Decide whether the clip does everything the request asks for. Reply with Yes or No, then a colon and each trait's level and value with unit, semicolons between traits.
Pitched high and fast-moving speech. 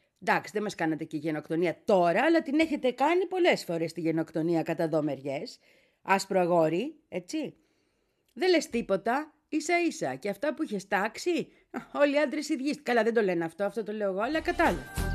Yes: high, 215 Hz; fast, 175 wpm